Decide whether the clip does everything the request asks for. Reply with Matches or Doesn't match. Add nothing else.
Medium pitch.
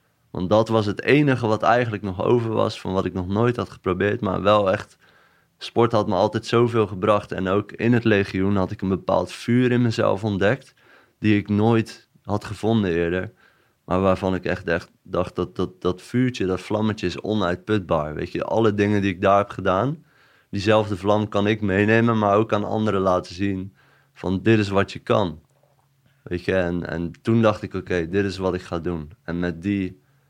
Doesn't match